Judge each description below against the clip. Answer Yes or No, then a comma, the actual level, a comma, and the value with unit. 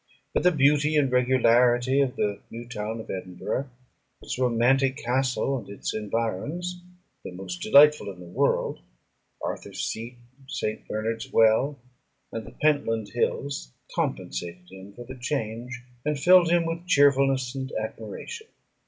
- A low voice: Yes, low, 125 Hz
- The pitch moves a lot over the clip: No, average, 4.3 semitones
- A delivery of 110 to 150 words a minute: Yes, average, 140 wpm